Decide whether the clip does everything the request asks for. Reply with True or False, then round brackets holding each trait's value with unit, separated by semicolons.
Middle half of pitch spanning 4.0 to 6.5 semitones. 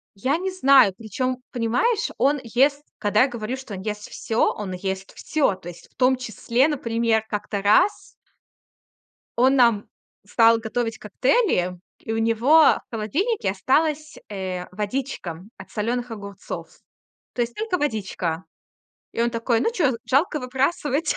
True (4.7 semitones)